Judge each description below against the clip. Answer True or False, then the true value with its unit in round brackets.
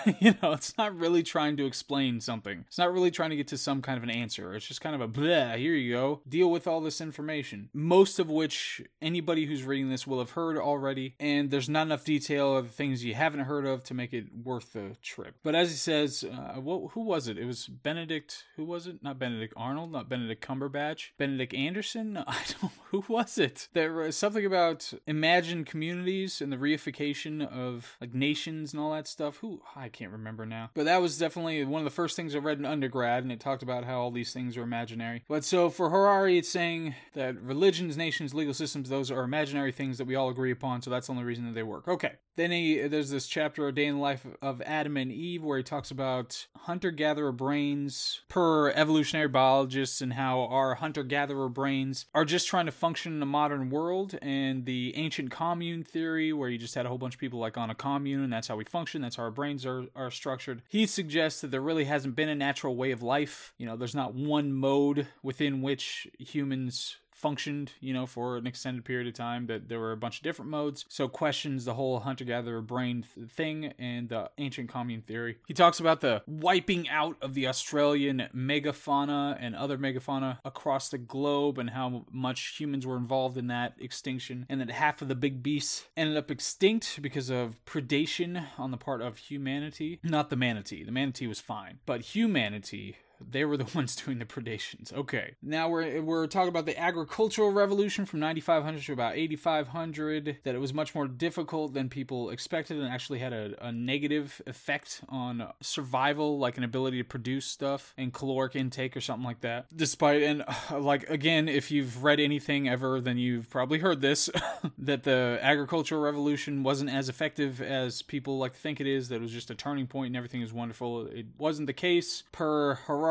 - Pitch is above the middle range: False (140 Hz)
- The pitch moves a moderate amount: True (3.4 semitones)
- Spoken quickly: True (210 wpm)